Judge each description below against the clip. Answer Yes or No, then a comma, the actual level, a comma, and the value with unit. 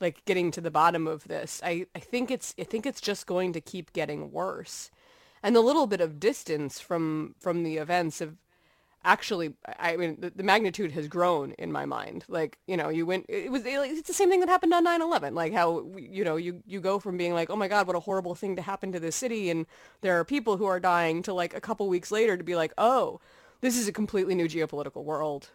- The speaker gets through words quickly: Yes, fast, 240 wpm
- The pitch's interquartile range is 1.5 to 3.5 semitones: No, average, 3.9 semitones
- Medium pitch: Yes, medium, 180 Hz